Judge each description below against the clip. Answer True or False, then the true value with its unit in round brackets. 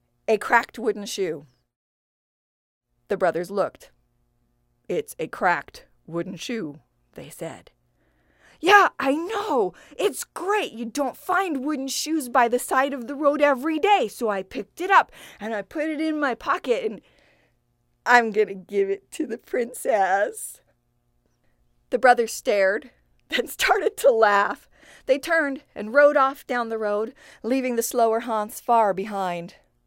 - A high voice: True (235 Hz)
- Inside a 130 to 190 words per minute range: True (150 wpm)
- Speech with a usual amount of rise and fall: False (8.9 semitones)